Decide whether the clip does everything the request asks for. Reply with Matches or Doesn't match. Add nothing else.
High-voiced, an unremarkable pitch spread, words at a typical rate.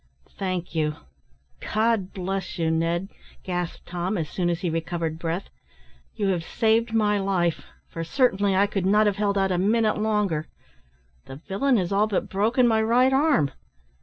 Matches